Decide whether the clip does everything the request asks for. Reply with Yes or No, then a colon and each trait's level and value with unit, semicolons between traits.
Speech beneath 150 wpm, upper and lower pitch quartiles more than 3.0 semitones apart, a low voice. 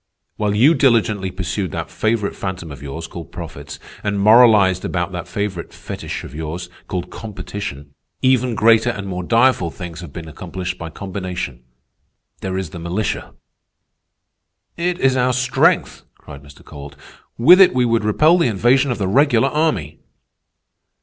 No: average, 155 wpm; wide, 5.6 semitones; low, 100 Hz